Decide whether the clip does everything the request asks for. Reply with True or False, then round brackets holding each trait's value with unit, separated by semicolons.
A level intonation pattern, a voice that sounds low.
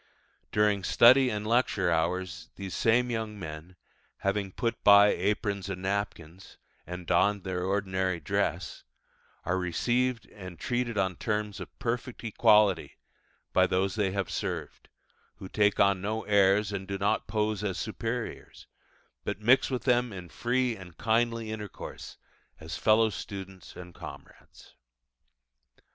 False (3.1 semitones; 100 Hz)